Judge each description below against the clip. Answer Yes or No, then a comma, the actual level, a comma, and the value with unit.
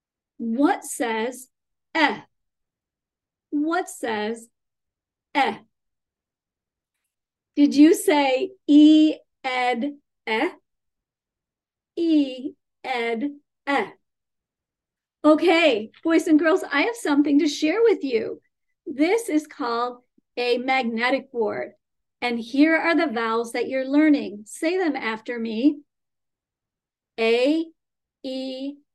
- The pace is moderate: No, slow, 95 wpm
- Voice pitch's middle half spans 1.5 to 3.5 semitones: No, average, 4.3 semitones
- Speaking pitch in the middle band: No, very high, 285 Hz